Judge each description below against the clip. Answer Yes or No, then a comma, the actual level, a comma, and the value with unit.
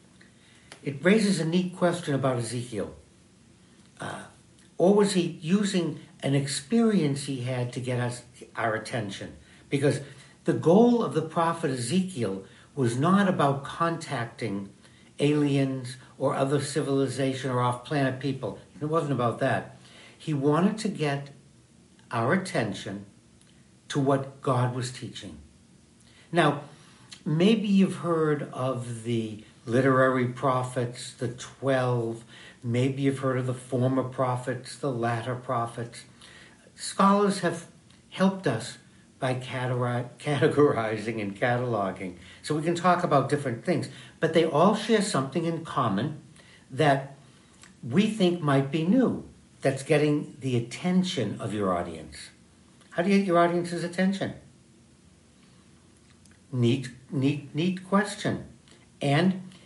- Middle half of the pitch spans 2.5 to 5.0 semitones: No, wide, 5.4 semitones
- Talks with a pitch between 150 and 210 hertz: No, low, 135 Hz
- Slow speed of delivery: Yes, slow, 120 wpm